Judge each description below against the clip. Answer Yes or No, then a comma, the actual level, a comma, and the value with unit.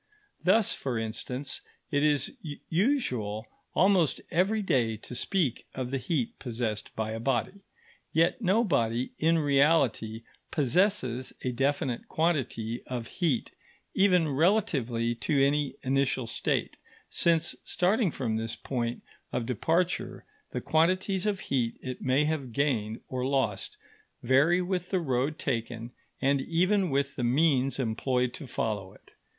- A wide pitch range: Yes, wide, 5.8 semitones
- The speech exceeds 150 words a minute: No, slow, 135 wpm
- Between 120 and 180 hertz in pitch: Yes, low, 135 Hz